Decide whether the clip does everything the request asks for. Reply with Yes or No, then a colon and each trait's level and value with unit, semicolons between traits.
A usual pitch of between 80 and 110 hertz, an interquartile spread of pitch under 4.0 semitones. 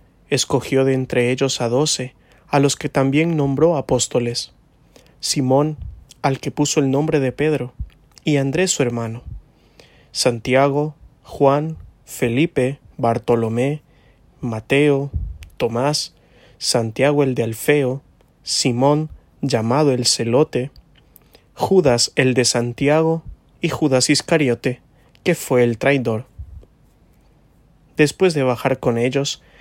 No: low, 135 Hz; average, 3.2 semitones